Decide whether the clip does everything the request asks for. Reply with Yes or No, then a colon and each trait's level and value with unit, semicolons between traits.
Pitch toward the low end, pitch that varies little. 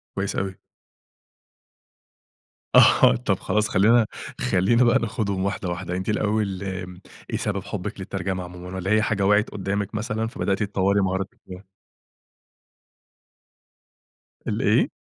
Yes: low, 100 Hz; narrow, 2.2 semitones